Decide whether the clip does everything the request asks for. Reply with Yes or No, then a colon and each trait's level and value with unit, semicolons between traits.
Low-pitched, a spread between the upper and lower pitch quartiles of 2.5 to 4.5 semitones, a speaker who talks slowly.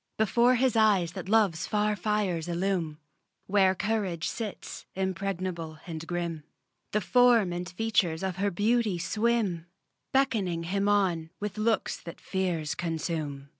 No: high, 190 Hz; average, 3.8 semitones; slow, 130 wpm